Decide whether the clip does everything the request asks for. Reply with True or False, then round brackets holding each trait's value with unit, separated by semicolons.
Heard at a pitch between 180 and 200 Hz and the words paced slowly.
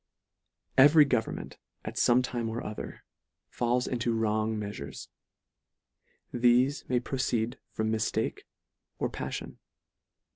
False (120 Hz; 110 wpm)